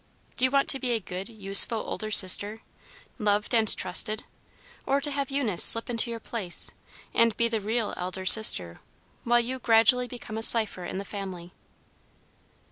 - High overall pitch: Yes, high, 225 Hz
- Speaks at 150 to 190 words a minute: Yes, average, 170 wpm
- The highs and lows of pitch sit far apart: No, average, 3.3 semitones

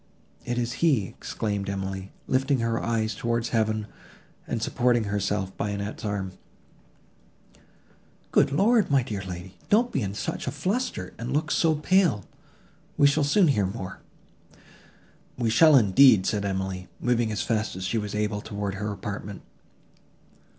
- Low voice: Yes, low, 110 Hz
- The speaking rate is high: No, average, 150 wpm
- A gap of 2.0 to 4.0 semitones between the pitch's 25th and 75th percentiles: No, average, 5.0 semitones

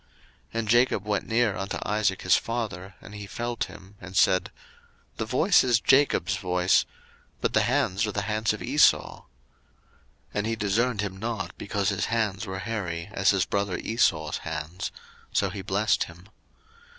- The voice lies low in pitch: Yes, low, 100 Hz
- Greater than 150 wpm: Yes, average, 170 wpm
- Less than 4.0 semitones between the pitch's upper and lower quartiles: Yes, average, 2.8 semitones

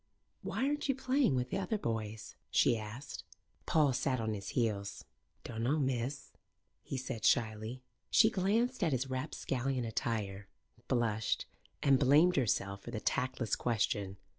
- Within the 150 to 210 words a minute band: No, average, 140 wpm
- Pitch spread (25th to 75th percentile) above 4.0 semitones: Yes, average, 4.7 semitones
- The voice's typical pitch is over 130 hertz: No, low, 125 Hz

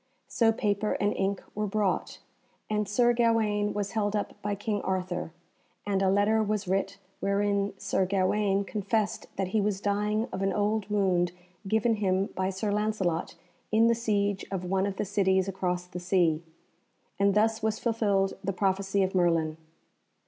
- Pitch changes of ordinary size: No, narrow, 1.8 semitones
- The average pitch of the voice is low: No, high, 200 Hz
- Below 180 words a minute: Yes, average, 165 wpm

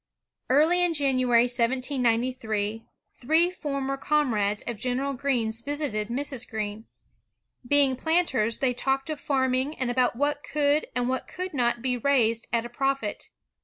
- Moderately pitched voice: No, very high, 255 Hz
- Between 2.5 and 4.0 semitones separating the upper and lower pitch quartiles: Yes, average, 3.4 semitones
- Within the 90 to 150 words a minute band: Yes, average, 145 wpm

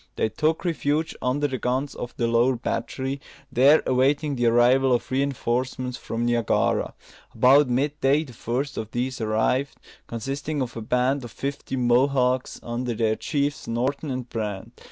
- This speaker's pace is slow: No, average, 155 wpm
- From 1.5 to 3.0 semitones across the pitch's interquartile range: Yes, average, 2.7 semitones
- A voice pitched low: Yes, low, 130 Hz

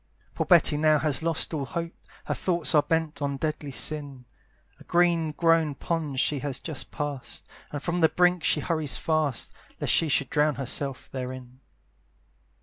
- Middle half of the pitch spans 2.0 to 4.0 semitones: Yes, average, 2.7 semitones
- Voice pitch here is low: No, medium, 150 Hz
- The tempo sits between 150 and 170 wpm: Yes, average, 165 wpm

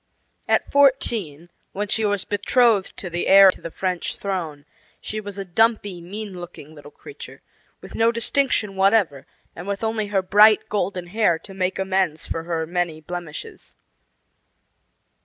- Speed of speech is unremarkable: Yes, average, 155 wpm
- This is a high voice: Yes, high, 195 Hz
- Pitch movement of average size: Yes, average, 3.4 semitones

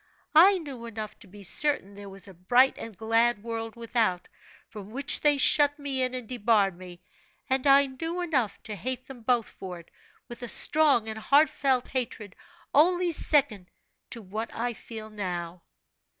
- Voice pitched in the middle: No, high, 235 Hz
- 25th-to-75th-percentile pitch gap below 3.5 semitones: No, average, 5.0 semitones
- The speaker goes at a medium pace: Yes, average, 170 wpm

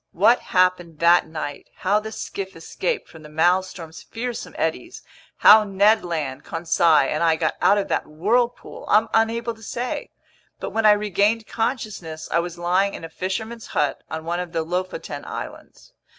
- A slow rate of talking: No, average, 170 wpm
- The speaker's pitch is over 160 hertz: Yes, medium, 185 Hz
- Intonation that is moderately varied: Yes, average, 4.9 semitones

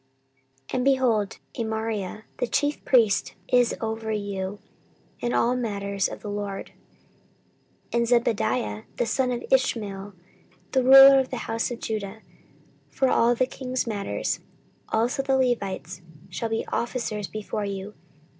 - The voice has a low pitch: No, high, 225 Hz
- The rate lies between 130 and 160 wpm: Yes, slow, 135 wpm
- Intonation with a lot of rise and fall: No, average, 3.6 semitones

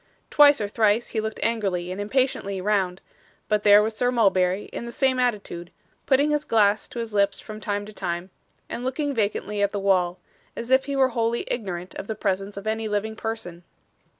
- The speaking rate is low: No, average, 200 wpm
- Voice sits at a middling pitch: No, high, 210 Hz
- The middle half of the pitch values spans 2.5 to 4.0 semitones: Yes, average, 3.1 semitones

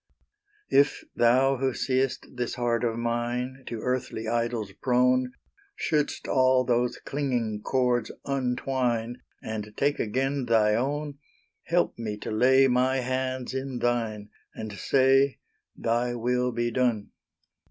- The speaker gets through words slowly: Yes, slow, 125 wpm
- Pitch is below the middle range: Yes, low, 125 Hz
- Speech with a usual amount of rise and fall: No, narrow, 2.0 semitones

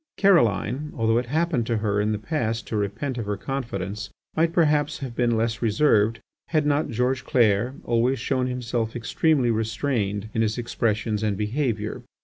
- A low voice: Yes, low, 115 Hz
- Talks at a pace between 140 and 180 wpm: Yes, average, 170 wpm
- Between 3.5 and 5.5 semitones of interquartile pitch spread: Yes, average, 3.8 semitones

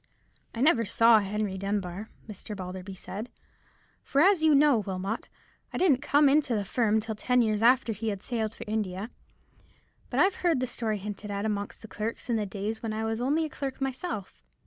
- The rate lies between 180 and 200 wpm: Yes, average, 190 wpm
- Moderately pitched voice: No, high, 220 Hz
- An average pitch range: Yes, average, 4.0 semitones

